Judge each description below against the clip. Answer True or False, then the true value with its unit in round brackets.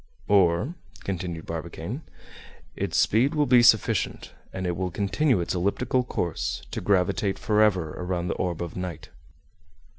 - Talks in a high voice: False (95 Hz)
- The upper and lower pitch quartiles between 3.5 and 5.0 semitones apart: True (3.9 semitones)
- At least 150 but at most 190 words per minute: False (140 wpm)